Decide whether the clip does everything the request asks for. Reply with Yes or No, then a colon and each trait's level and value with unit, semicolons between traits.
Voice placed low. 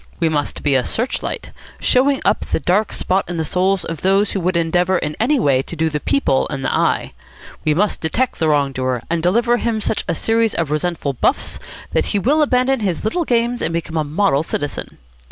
No: medium, 180 Hz